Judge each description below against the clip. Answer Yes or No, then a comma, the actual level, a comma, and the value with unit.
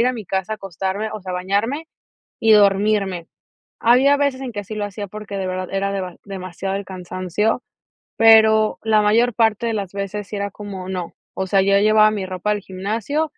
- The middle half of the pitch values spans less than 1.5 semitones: No, narrow, 2.4 semitones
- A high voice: Yes, high, 205 Hz